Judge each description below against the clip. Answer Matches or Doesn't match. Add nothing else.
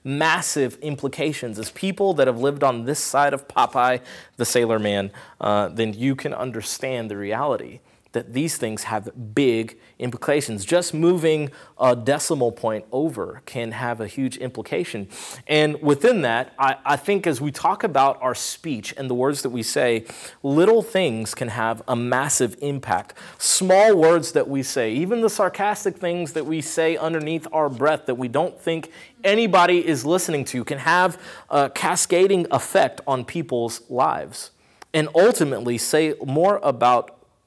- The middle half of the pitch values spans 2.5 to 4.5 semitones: Doesn't match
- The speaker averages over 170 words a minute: Doesn't match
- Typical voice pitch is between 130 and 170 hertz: Matches